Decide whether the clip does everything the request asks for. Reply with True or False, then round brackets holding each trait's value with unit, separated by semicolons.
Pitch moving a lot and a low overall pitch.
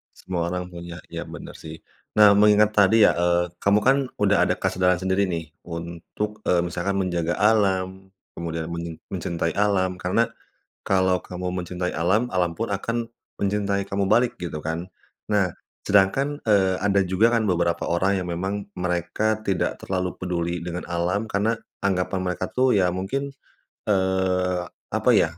False (2.7 semitones; 95 Hz)